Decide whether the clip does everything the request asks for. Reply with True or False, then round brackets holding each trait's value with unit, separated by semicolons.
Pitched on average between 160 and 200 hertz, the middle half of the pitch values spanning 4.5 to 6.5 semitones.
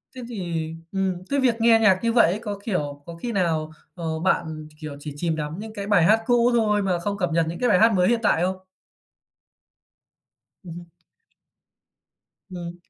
True (185 Hz; 4.8 semitones)